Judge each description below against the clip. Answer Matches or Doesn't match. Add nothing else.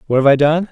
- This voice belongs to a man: Matches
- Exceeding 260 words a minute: Matches